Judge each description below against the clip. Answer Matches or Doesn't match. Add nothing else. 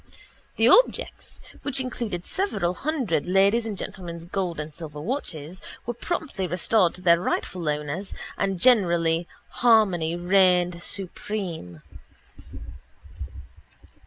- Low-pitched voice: Doesn't match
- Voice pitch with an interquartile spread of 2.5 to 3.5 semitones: Doesn't match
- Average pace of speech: Doesn't match